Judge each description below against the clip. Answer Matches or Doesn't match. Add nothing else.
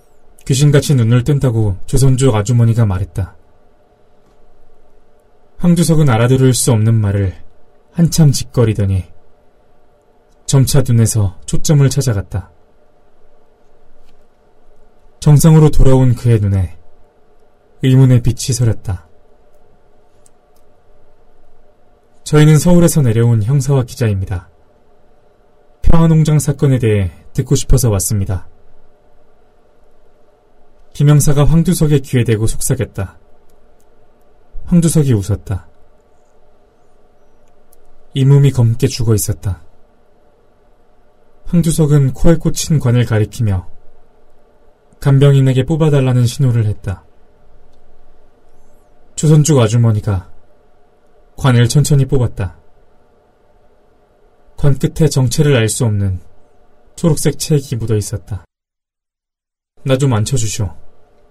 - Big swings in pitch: Matches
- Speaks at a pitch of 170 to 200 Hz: Doesn't match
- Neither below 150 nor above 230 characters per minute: Matches